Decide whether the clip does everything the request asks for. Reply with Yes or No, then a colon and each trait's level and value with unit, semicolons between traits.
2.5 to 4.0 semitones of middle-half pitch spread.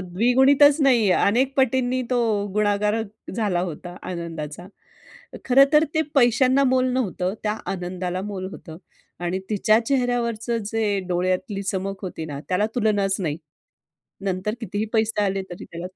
No: average, 5.0 semitones